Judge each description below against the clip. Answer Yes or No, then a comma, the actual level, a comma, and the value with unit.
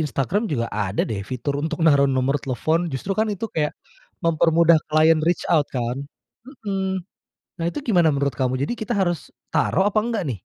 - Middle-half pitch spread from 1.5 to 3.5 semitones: No, wide, 5.5 semitones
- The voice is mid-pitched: Yes, medium, 160 Hz